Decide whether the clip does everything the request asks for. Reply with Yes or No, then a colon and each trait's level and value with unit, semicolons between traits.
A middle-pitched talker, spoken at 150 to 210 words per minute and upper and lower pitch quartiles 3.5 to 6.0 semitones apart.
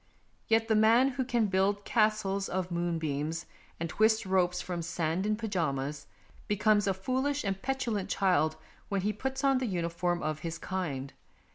No: high, 195 Hz; average, 165 wpm; average, 4.3 semitones